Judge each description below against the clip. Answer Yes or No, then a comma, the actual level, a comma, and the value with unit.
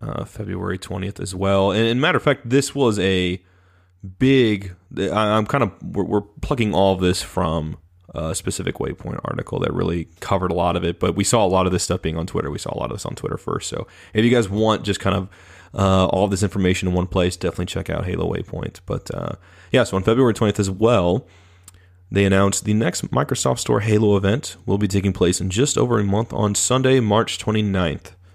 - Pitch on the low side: Yes, very low, 95 Hz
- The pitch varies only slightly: No, average, 3.0 semitones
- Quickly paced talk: Yes, fast, 220 wpm